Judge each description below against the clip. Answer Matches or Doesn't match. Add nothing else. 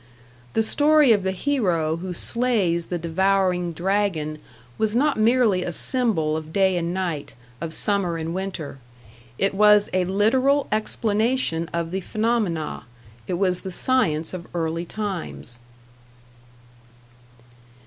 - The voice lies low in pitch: Doesn't match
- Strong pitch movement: Doesn't match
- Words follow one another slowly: Matches